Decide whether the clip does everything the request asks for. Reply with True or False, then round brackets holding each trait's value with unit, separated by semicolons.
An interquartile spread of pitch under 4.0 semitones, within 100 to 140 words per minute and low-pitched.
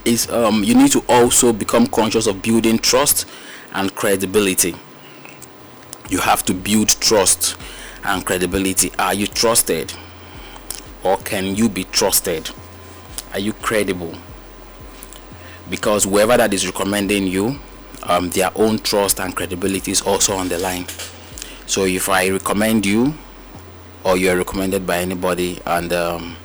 True (2.9 semitones; 135 wpm; 95 Hz)